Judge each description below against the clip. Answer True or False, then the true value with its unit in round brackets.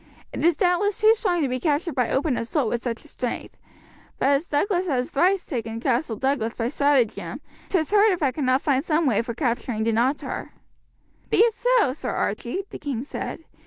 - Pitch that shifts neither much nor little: False (6.2 semitones)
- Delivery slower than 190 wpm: False (195 wpm)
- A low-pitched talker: False (280 Hz)